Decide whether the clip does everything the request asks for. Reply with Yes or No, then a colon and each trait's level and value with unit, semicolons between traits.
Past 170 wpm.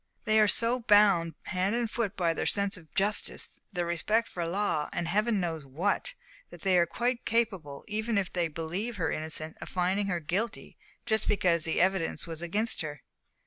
Yes: average, 185 wpm